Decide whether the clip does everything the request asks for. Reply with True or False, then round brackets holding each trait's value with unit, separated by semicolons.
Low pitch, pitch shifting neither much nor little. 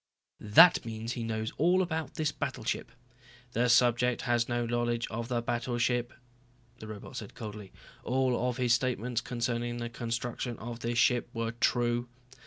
False (120 Hz; 1.1 semitones)